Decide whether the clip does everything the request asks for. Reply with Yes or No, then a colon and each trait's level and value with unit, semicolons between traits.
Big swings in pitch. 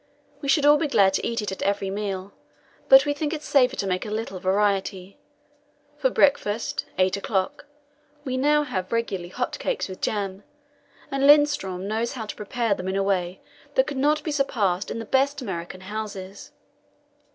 Yes: wide, 6.3 semitones